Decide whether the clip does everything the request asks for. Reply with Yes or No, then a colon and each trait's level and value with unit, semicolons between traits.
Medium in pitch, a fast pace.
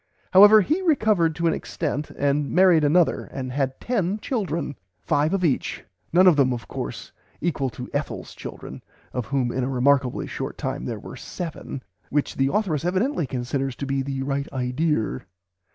No: medium, 145 Hz; average, 170 wpm